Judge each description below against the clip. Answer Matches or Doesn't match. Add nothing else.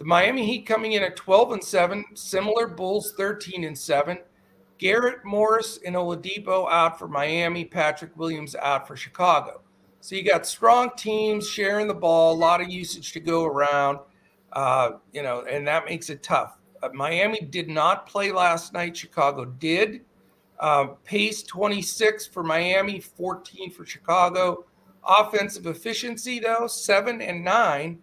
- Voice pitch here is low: Doesn't match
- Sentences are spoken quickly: Doesn't match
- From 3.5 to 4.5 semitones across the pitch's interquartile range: Matches